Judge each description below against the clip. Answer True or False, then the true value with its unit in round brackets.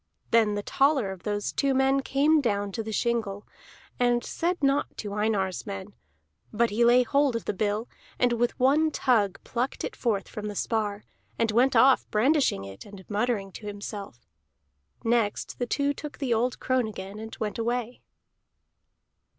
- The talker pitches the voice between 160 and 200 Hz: False (230 Hz)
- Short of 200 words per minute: True (170 wpm)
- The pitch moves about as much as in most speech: True (3.9 semitones)